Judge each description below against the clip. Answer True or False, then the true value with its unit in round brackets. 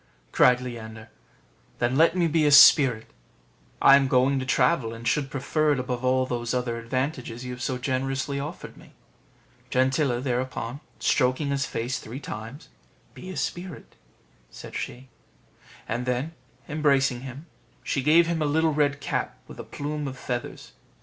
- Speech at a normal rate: True (160 wpm)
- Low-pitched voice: True (130 Hz)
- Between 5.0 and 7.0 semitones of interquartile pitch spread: False (2.9 semitones)